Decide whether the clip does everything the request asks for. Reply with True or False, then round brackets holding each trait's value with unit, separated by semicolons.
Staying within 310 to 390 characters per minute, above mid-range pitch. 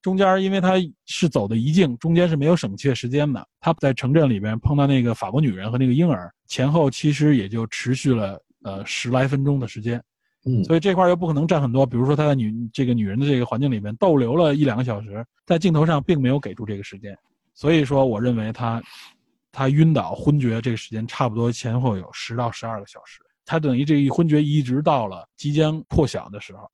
False (345 characters per minute; 135 Hz)